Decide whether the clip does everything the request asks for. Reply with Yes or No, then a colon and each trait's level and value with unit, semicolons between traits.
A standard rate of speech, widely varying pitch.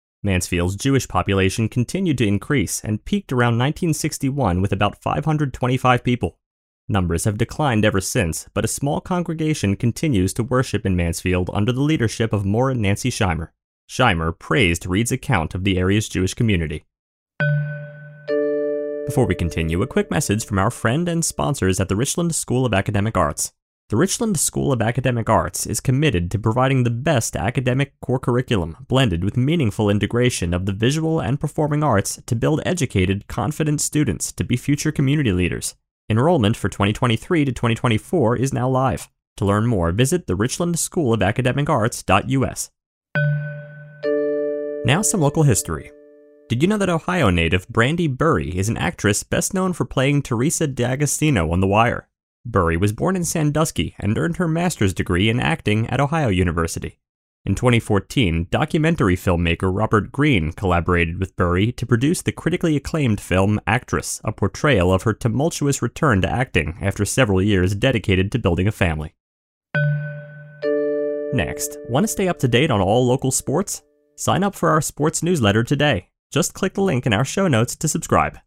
Yes: average, 165 wpm; wide, 7.0 semitones